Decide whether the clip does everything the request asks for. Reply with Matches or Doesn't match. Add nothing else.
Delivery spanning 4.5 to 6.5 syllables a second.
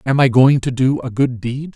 Matches